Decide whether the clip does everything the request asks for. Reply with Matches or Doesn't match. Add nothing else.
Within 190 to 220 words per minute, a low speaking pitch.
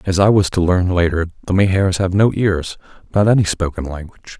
Matches